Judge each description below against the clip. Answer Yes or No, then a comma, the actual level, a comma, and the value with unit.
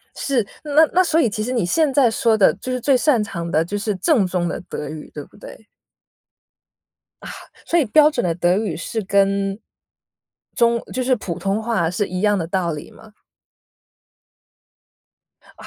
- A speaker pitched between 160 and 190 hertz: No, high, 210 Hz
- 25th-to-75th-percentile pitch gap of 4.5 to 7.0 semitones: Yes, wide, 5.5 semitones